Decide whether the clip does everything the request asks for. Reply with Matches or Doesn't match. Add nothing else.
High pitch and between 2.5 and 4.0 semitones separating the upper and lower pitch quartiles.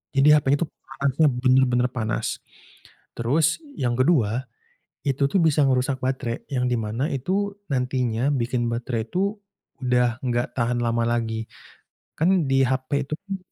Doesn't match